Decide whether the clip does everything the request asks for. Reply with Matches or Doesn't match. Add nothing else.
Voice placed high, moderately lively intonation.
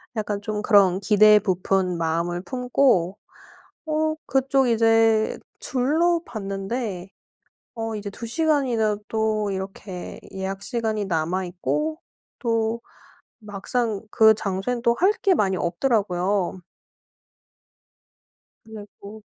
Matches